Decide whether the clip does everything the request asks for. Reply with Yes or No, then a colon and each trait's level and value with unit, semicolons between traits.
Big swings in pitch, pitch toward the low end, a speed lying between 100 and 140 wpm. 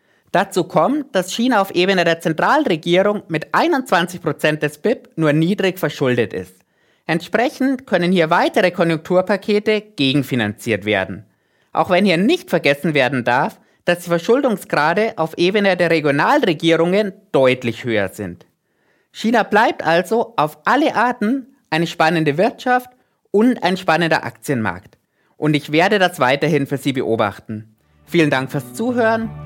No: wide, 6.3 semitones; medium, 170 Hz; average, 130 wpm